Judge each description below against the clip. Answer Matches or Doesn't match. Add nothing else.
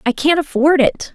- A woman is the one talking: Matches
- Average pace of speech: Doesn't match